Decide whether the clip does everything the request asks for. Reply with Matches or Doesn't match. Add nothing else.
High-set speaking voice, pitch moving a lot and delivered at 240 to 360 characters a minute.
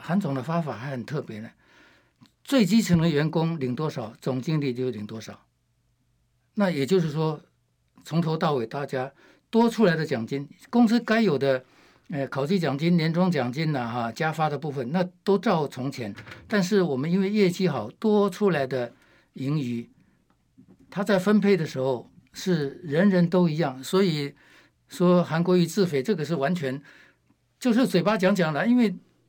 Doesn't match